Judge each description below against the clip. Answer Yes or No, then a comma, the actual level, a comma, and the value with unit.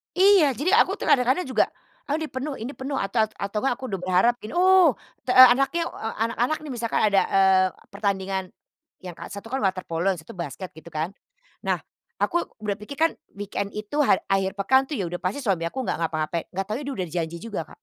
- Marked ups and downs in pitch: Yes, wide, 6.0 semitones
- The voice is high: Yes, high, 215 Hz